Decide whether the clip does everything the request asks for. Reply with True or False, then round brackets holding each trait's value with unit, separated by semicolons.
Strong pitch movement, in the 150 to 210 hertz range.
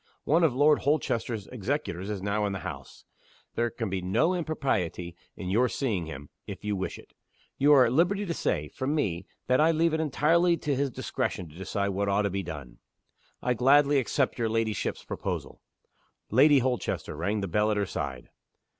False (6.8 semitones; 115 Hz)